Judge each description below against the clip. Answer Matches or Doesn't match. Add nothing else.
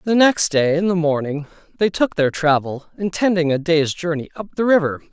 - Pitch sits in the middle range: Matches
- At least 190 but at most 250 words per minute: Matches